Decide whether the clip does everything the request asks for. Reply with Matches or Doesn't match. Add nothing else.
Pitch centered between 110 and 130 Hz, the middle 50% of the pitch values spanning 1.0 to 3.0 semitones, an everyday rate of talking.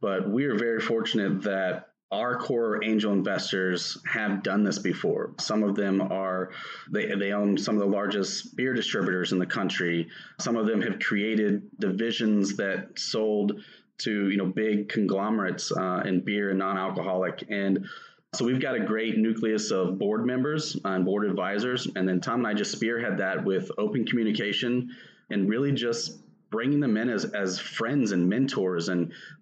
Doesn't match